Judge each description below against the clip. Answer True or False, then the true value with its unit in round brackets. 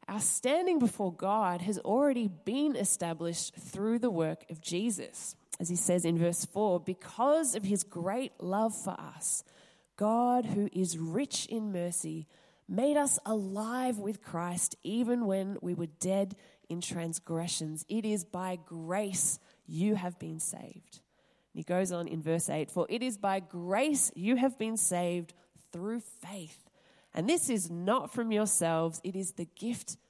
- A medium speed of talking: True (160 wpm)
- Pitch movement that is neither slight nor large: True (4.3 semitones)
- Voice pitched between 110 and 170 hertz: False (190 Hz)